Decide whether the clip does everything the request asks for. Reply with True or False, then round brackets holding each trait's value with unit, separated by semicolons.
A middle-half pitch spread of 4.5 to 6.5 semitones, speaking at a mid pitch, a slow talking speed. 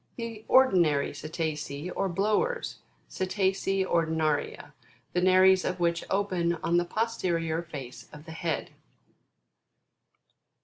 False (3.2 semitones; 175 Hz; 105 wpm)